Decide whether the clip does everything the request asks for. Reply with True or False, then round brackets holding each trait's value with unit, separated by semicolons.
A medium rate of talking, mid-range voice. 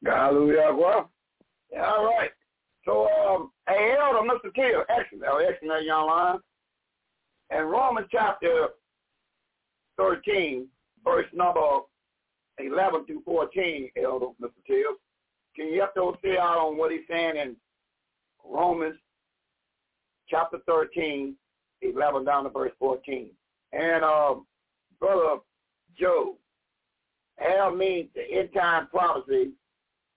False (105 wpm; 175 Hz)